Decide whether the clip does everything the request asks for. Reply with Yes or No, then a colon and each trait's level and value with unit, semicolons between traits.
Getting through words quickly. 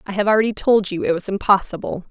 Yes: fast, 230 wpm